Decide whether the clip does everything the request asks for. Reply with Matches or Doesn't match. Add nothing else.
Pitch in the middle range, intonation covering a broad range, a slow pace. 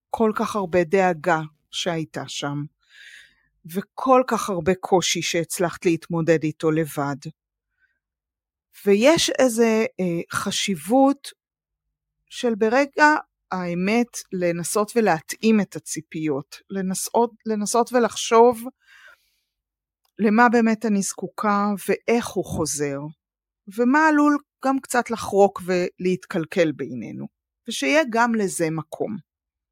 Doesn't match